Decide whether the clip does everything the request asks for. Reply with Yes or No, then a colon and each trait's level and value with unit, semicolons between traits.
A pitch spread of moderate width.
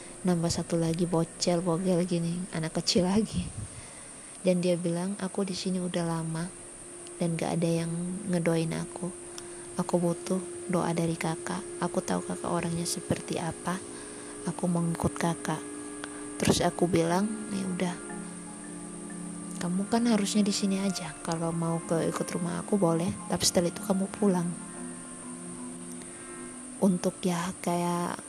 No: narrow, 1.8 semitones